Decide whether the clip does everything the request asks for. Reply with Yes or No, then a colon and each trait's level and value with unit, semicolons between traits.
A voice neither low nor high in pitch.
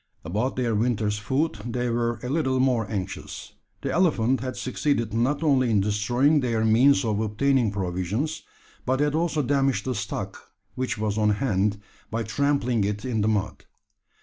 No: low, 120 Hz